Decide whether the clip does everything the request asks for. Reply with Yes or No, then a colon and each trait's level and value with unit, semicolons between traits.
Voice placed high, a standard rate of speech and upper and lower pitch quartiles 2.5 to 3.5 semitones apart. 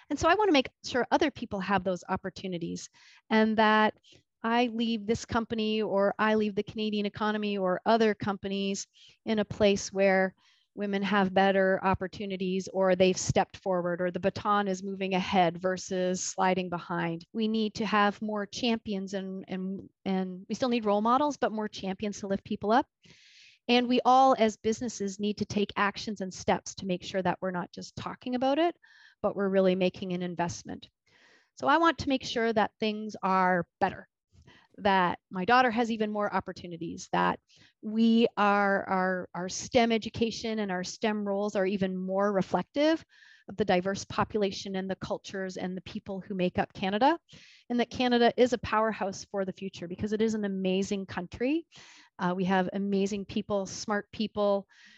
Yes: high, 200 Hz; average, 180 wpm; average, 2.8 semitones